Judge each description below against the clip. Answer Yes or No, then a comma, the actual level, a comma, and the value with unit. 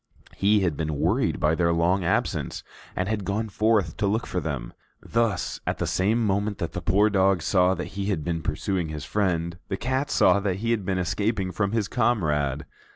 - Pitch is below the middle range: Yes, very low, 95 Hz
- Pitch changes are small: No, average, 3.8 semitones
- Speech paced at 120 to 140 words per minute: No, fast, 205 wpm